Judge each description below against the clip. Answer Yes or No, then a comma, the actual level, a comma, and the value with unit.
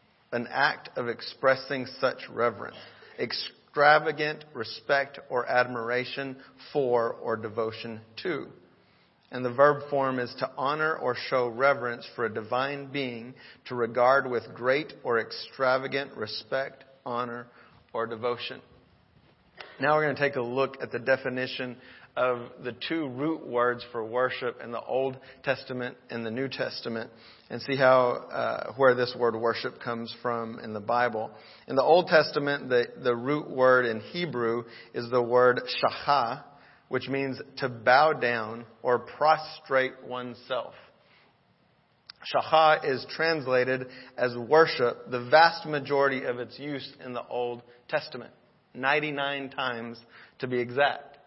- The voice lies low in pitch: Yes, low, 130 Hz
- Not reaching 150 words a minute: Yes, average, 140 wpm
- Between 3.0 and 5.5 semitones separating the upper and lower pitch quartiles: No, narrow, 2.5 semitones